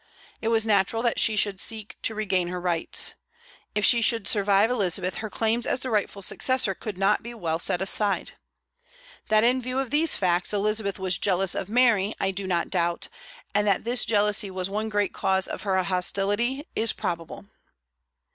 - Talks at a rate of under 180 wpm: No, average, 185 wpm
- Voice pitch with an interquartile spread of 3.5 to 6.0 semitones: No, average, 3.0 semitones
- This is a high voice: Yes, high, 205 Hz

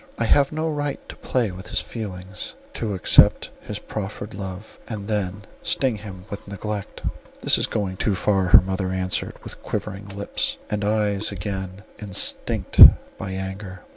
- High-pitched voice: No, low, 100 Hz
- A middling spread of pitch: No, narrow, 2.1 semitones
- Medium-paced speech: Yes, average, 160 wpm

